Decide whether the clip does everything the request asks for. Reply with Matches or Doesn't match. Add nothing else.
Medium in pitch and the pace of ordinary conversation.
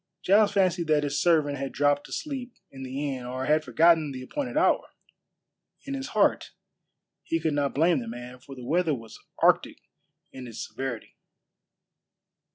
Matches